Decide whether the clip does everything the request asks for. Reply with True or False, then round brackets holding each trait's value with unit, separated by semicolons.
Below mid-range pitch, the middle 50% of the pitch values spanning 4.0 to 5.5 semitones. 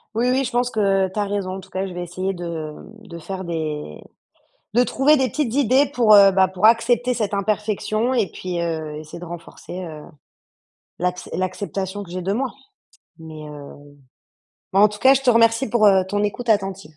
False (195 Hz; 4.4 semitones)